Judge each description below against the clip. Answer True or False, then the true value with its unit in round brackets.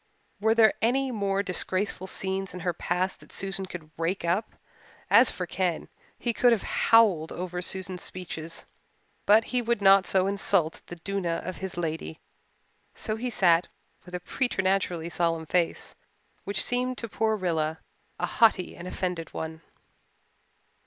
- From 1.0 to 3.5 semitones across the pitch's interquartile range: True (3.2 semitones)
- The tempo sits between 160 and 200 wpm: False (150 wpm)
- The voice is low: False (185 Hz)